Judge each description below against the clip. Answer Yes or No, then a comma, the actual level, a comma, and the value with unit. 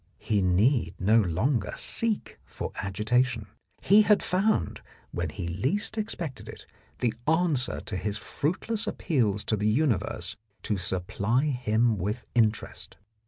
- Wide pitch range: Yes, wide, 7.0 semitones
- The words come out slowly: Yes, slow, 130 wpm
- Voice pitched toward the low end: Yes, low, 115 Hz